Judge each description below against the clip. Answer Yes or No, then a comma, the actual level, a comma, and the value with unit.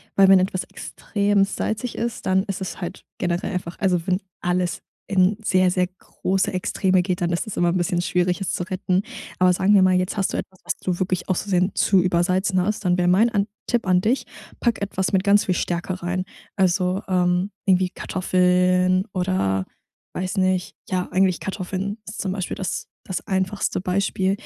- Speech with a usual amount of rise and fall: No, narrow, 1.2 semitones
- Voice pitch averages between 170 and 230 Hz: Yes, medium, 185 Hz